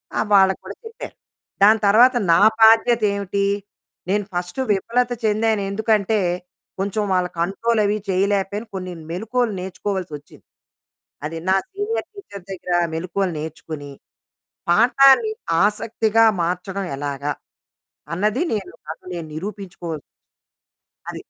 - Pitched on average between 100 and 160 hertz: No, high, 200 Hz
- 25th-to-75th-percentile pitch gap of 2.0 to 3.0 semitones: No, average, 3.7 semitones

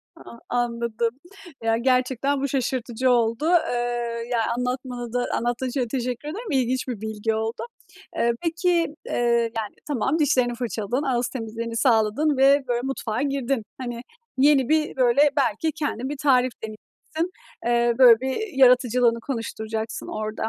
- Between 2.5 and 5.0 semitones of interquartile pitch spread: Yes, average, 2.8 semitones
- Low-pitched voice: No, high, 245 Hz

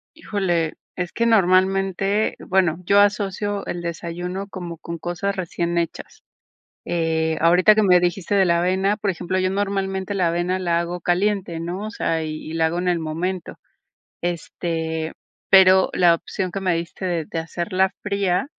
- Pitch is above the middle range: No, medium, 180 Hz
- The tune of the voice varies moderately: No, narrow, 2.3 semitones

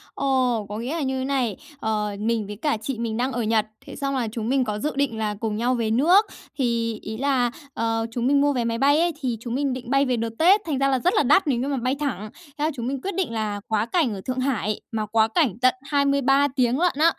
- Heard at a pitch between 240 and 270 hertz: Yes, very high, 250 Hz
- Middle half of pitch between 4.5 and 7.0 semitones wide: No, average, 3.7 semitones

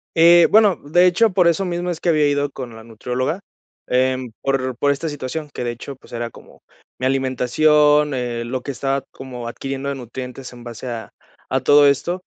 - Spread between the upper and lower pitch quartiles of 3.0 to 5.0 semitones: Yes, average, 3.5 semitones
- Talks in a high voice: No, low, 135 Hz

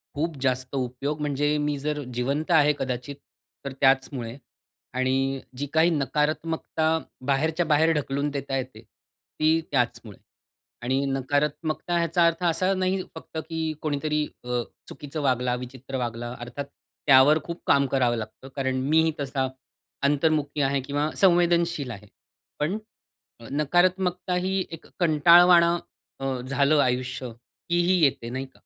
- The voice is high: No, medium, 145 Hz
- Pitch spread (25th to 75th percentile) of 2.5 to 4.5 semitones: Yes, average, 3.6 semitones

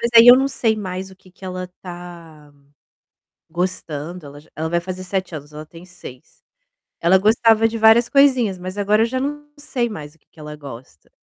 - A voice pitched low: No, medium, 185 Hz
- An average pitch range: No, wide, 5.8 semitones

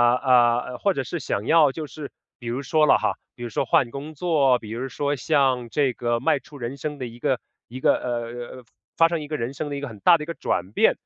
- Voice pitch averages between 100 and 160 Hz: Yes, low, 135 Hz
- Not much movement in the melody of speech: No, average, 3.6 semitones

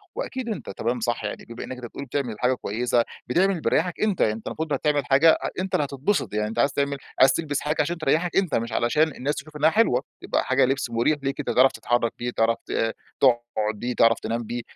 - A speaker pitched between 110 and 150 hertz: Yes, low, 135 Hz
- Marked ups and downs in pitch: No, average, 4.5 semitones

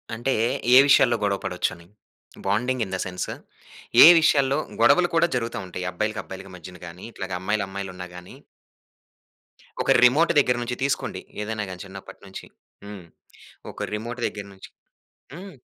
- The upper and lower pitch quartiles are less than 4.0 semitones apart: No, average, 4.9 semitones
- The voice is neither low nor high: No, low, 105 Hz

